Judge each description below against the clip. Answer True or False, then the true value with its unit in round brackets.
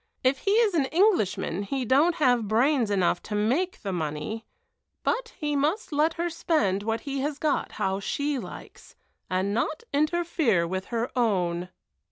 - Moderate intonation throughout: False (7.5 semitones)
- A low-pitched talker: False (255 Hz)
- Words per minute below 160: False (165 wpm)